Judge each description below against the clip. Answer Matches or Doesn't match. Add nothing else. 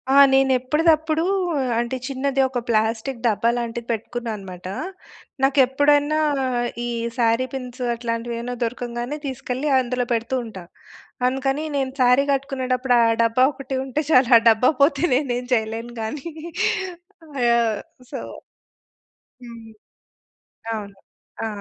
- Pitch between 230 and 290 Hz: Matches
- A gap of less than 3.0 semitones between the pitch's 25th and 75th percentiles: Matches